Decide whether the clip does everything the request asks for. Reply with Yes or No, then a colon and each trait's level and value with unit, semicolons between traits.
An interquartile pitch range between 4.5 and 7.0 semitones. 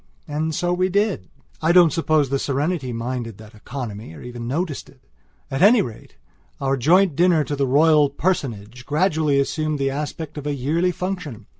Yes: average, 4.8 semitones